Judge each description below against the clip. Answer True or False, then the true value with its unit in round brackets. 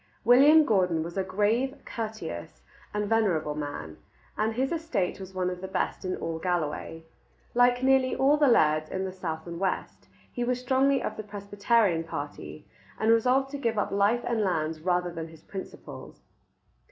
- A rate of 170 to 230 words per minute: True (175 wpm)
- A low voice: False (200 Hz)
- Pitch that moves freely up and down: True (6.4 semitones)